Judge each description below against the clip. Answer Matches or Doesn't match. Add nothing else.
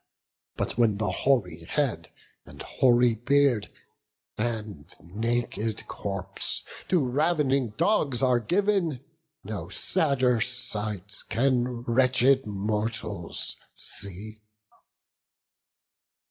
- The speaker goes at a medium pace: Doesn't match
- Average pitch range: Matches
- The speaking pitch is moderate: Doesn't match